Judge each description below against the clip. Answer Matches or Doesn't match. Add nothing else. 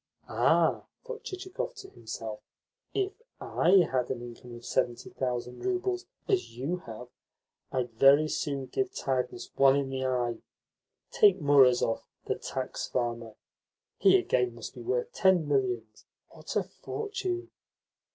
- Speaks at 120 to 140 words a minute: Matches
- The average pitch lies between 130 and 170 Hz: Matches